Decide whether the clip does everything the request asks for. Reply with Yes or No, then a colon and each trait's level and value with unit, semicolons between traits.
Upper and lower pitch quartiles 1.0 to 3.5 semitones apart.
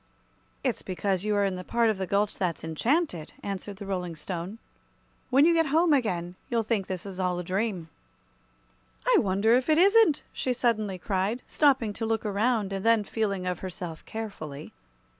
No: average, 4.1 semitones